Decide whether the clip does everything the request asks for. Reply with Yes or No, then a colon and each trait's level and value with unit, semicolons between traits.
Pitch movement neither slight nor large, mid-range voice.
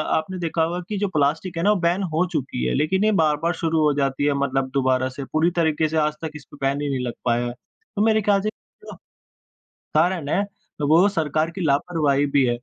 Yes: average, 3.7 semitones; medium, 155 Hz